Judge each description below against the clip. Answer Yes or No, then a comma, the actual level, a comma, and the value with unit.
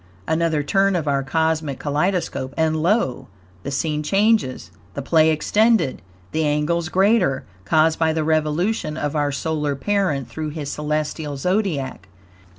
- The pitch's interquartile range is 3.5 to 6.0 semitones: No, average, 3.0 semitones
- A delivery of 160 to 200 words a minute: No, average, 140 wpm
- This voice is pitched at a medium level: Yes, medium, 155 Hz